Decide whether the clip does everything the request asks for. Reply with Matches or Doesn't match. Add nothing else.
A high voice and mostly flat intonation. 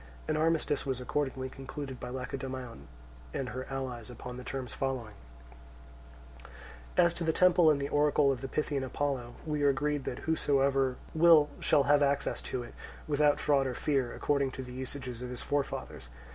Doesn't match